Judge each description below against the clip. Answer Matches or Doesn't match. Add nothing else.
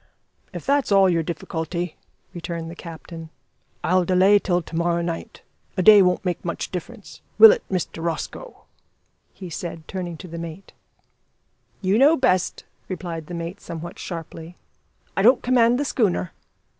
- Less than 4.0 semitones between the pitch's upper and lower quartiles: Matches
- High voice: Doesn't match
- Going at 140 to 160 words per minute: Matches